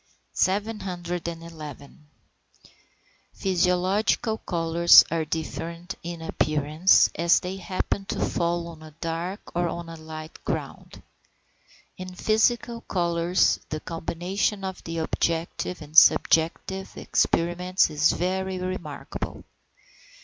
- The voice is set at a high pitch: No, medium, 170 Hz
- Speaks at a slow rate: Yes, slow, 100 wpm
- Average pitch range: No, narrow, 2.2 semitones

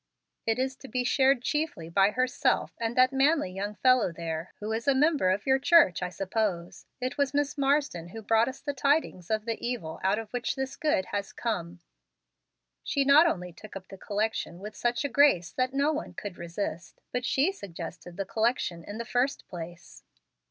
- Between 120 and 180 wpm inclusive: No, average, 195 wpm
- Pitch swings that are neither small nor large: No, wide, 6.5 semitones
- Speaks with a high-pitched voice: Yes, high, 225 Hz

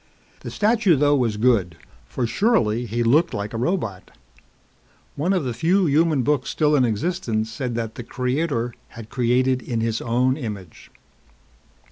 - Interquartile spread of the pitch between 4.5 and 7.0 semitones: Yes, average, 4.8 semitones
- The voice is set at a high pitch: No, low, 125 Hz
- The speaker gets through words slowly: No, average, 155 wpm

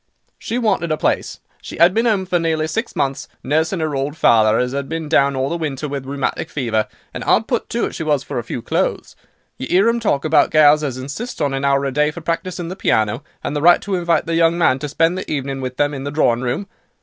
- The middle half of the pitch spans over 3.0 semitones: Yes, average, 3.8 semitones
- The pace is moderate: No, fast, 255 wpm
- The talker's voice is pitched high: No, medium, 150 Hz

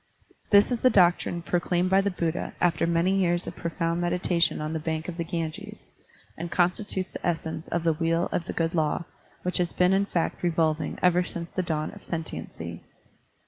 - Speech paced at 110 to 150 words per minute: No, average, 190 wpm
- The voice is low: No, medium, 170 Hz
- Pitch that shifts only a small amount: Yes, narrow, 1.7 semitones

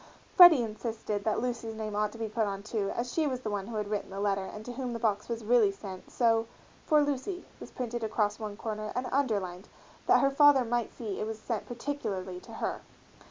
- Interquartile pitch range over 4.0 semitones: No, average, 2.9 semitones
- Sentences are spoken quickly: Yes, fast, 225 wpm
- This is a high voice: Yes, high, 225 Hz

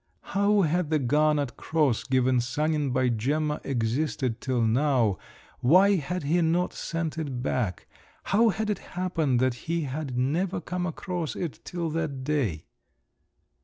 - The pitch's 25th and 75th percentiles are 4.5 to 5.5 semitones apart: Yes, average, 4.8 semitones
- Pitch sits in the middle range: Yes, medium, 150 Hz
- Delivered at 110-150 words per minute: Yes, average, 145 wpm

